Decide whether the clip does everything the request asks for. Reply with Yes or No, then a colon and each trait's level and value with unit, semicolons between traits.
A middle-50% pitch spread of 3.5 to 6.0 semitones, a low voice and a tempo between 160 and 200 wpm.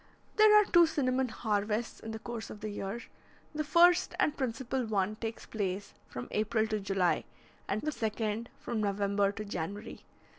No: average, 3.9 semitones; high, 220 Hz; average, 170 wpm